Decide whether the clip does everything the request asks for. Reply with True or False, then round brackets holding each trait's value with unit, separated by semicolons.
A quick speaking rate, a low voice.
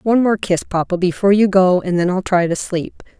False (245 wpm; 190 Hz)